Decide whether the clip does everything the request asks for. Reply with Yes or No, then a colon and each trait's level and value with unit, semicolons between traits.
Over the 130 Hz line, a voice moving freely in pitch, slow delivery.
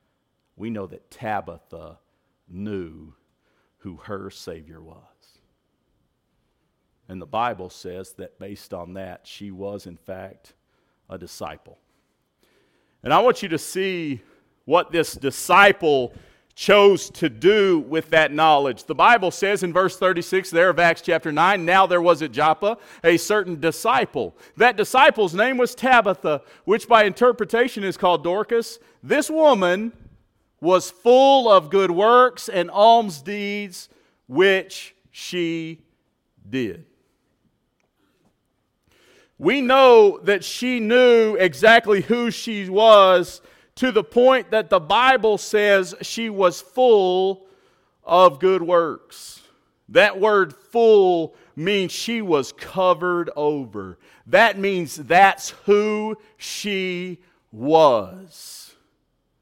No: high, 190 Hz; average, 5.0 semitones; slow, 120 wpm